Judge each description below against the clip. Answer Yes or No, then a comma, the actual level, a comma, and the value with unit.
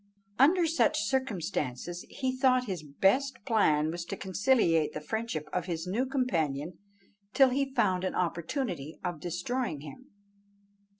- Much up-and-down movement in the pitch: Yes, wide, 7.9 semitones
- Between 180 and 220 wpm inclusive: No, slow, 135 wpm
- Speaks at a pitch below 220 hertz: Yes, medium, 185 Hz